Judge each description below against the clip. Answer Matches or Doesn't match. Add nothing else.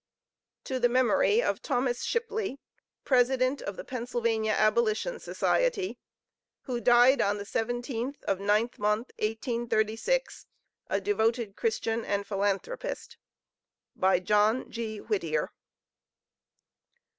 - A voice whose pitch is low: Doesn't match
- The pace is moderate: Doesn't match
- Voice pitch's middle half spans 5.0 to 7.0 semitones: Doesn't match